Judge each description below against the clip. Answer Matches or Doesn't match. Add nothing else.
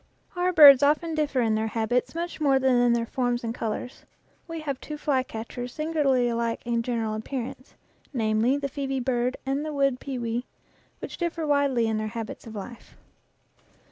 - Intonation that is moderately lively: Matches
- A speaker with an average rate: Matches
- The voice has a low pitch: Doesn't match